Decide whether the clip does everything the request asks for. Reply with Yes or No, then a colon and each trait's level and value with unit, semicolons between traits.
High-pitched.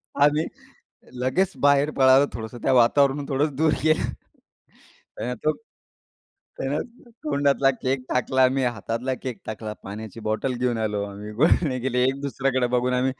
No: low, 130 Hz